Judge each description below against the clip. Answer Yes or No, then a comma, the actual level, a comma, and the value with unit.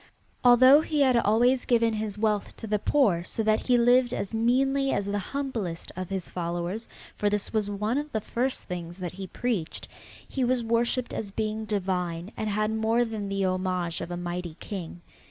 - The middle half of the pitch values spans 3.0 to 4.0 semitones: No, average, 4.6 semitones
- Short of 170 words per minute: No, average, 190 wpm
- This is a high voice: Yes, high, 215 Hz